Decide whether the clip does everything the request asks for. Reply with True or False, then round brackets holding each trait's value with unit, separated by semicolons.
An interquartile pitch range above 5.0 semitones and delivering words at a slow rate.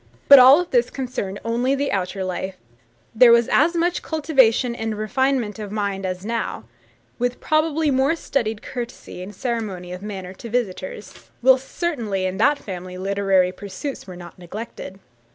False (5.5 semitones; 155 wpm)